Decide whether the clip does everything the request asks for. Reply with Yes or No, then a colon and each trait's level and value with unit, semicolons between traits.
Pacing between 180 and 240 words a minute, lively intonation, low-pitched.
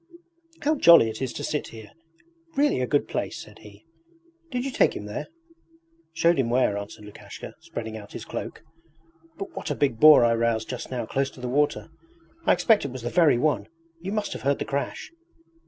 Yes: fast, 205 wpm; wide, 6.4 semitones; low, 130 Hz